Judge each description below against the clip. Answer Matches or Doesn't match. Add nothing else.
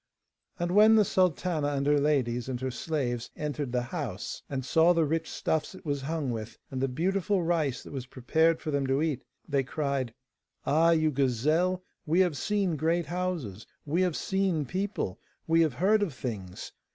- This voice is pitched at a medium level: Matches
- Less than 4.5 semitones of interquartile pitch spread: Doesn't match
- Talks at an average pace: Matches